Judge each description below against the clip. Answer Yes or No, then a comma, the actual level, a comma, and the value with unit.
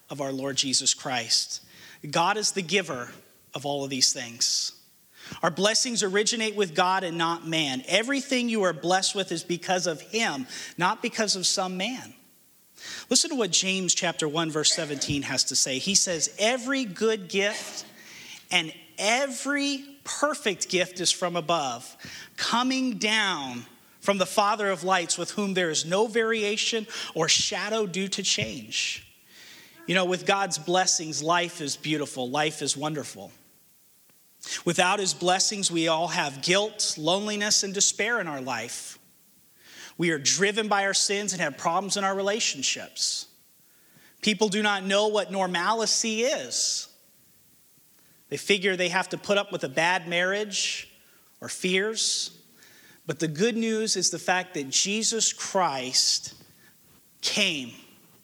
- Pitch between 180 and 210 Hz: Yes, high, 190 Hz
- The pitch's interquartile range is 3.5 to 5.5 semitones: Yes, average, 4.1 semitones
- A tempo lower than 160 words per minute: Yes, average, 150 wpm